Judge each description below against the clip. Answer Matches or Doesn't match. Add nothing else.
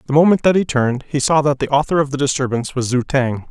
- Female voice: Doesn't match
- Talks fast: Matches